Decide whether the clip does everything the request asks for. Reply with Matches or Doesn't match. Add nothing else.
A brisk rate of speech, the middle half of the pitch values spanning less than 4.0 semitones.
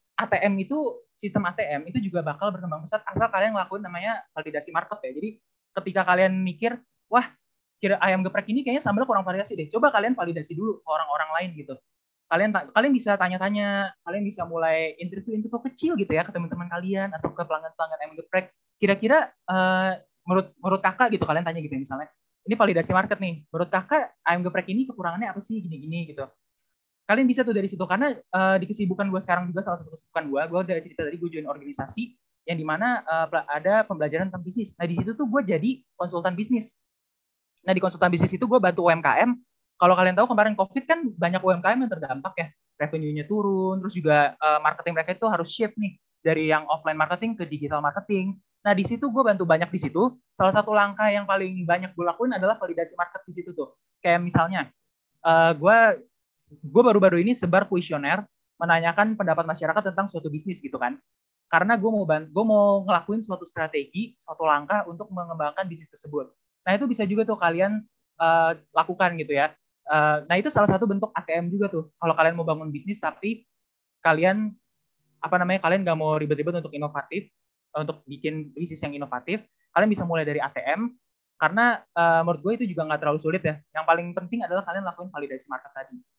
Doesn't match